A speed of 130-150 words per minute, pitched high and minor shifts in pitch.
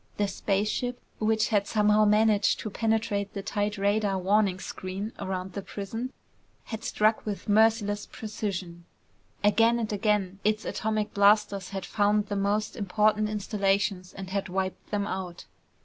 Yes: average, 145 wpm; high, 205 Hz; narrow, 1.5 semitones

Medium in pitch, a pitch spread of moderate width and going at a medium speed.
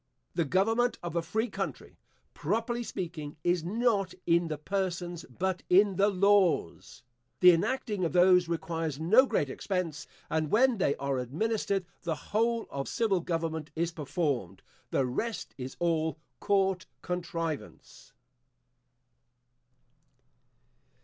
No: medium, 175 Hz; average, 3.9 semitones; slow, 125 wpm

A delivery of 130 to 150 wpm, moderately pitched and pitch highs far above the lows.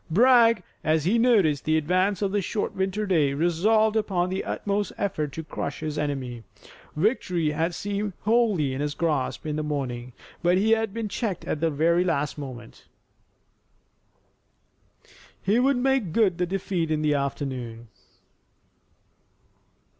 Yes: average, 145 wpm; medium, 175 Hz; wide, 5.7 semitones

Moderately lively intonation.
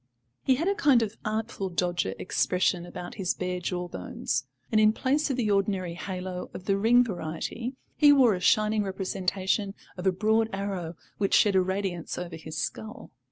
Yes: average, 3.4 semitones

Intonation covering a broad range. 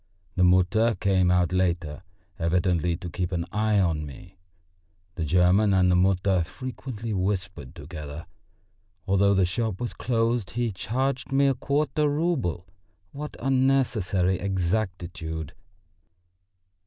No: average, 4.6 semitones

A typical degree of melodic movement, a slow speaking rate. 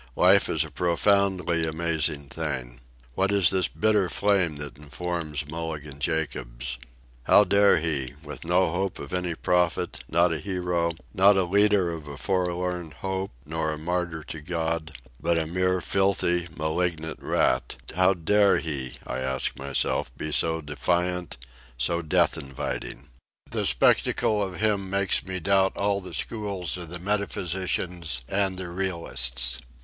No: average, 3.4 semitones; average, 145 wpm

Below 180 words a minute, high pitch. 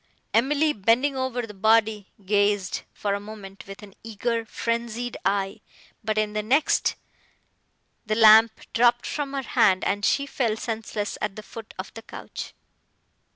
Yes: average, 155 wpm; high, 220 Hz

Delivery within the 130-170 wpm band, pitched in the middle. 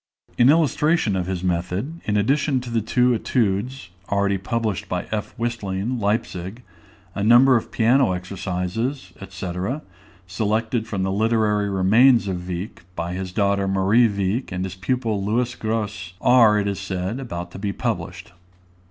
No: average, 150 wpm; low, 105 Hz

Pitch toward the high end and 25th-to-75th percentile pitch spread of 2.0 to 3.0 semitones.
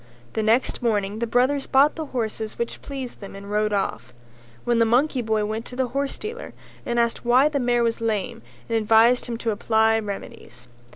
Yes: high, 230 Hz; narrow, 2.6 semitones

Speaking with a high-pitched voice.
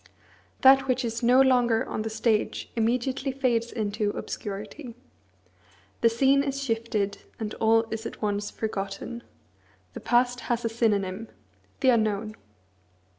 Yes: high, 230 Hz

